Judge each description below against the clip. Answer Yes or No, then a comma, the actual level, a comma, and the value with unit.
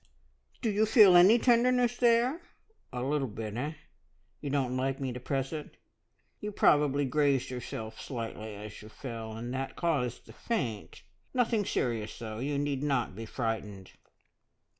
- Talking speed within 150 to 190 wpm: Yes, average, 155 wpm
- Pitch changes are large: Yes, wide, 7.3 semitones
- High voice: No, low, 135 Hz